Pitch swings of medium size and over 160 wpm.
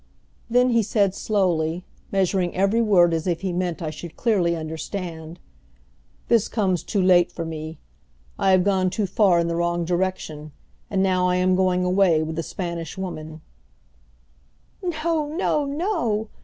No: average, 3.1 semitones; average, 155 wpm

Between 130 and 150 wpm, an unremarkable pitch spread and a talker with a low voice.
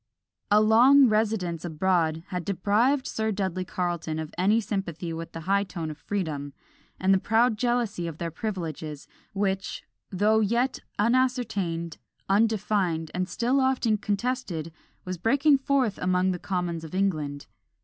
No: average, 140 wpm; average, 4.7 semitones; high, 195 Hz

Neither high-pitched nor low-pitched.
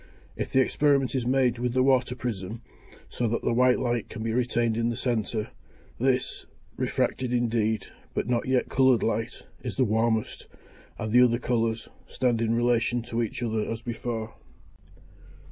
No: low, 120 Hz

